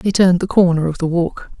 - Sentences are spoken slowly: No, fast, 265 wpm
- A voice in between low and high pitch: Yes, medium, 175 Hz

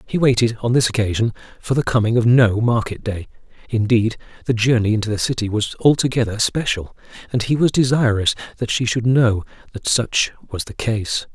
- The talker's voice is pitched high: No, low, 115 Hz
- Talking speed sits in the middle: Yes, average, 180 wpm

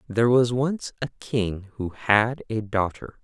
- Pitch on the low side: Yes, low, 115 Hz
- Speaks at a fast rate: No, average, 165 wpm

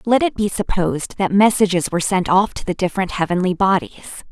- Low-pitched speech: No, high, 190 Hz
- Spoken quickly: No, average, 195 wpm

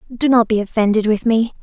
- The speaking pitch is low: No, high, 225 Hz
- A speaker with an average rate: No, fast, 220 wpm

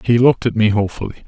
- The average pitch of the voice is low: Yes, low, 115 Hz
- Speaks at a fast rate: Yes, fast, 235 wpm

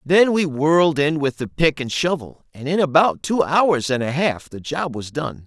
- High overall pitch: No, medium, 150 Hz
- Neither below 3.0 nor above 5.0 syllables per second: Yes, 4.5 syllables/s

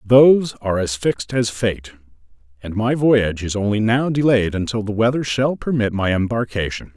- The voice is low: Yes, low, 110 Hz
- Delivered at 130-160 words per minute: No, average, 170 wpm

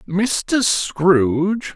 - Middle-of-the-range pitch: Yes, medium, 180 Hz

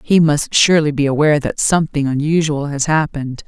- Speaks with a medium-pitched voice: Yes, medium, 150 Hz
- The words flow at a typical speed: Yes, average, 175 wpm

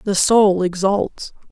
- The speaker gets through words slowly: Yes, slow, 120 wpm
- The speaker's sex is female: Yes, female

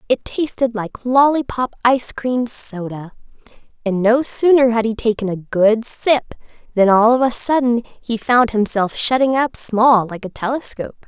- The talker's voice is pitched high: Yes, high, 235 Hz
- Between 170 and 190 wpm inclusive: No, average, 160 wpm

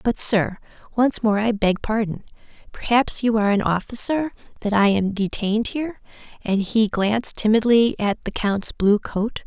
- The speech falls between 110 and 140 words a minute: No, average, 165 wpm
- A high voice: Yes, high, 215 Hz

